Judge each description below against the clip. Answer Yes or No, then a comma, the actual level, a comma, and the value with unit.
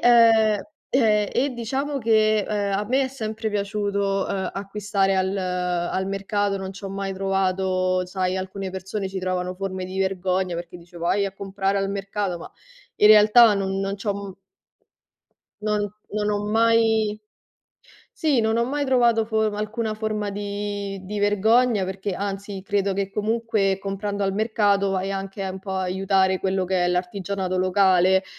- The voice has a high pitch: Yes, high, 195 Hz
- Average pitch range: No, narrow, 2.0 semitones